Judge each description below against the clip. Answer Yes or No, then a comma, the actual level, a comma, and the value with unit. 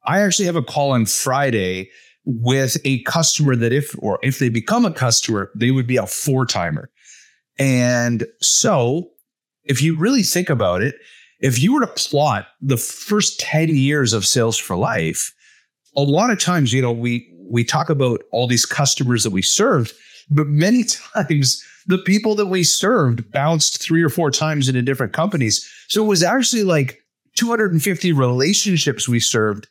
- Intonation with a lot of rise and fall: Yes, wide, 6.3 semitones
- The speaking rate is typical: Yes, average, 175 wpm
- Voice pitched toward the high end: No, medium, 140 Hz